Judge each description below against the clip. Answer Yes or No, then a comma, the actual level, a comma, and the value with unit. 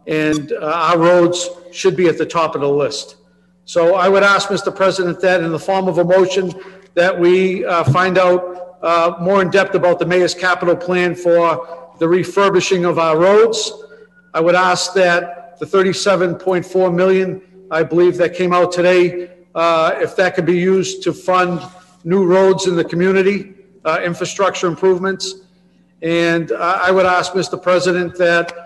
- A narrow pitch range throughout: Yes, narrow, 1.5 semitones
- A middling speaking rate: Yes, average, 170 wpm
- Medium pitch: Yes, medium, 180 Hz